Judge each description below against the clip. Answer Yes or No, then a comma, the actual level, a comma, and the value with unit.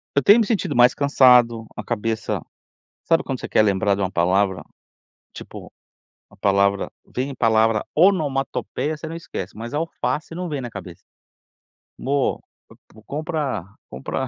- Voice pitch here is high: No, low, 125 Hz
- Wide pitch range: Yes, wide, 6.6 semitones